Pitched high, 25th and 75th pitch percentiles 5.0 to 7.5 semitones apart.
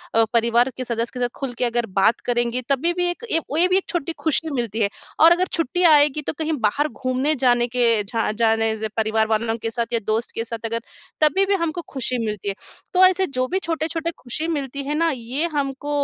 Yes: very high, 255 Hz; wide, 5.6 semitones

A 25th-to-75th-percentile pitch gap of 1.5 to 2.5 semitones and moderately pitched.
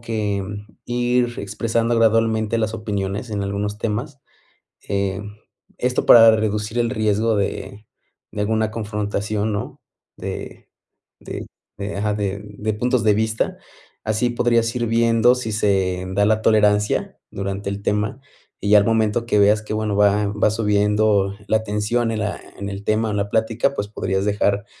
No: narrow, 1.8 semitones; low, 105 Hz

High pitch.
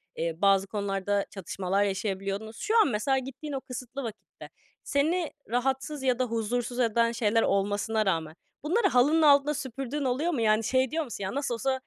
Yes: high, 240 Hz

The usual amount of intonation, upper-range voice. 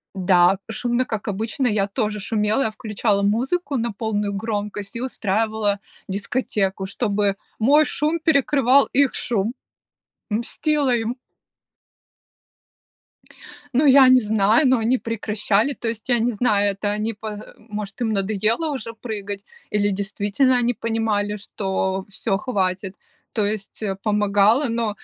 Yes: average, 3.0 semitones; high, 215 Hz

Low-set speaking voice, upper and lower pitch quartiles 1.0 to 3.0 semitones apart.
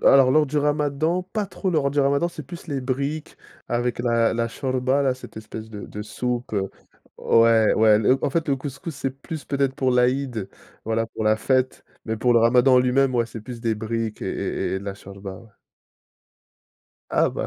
No: low, 125 Hz; average, 3.6 semitones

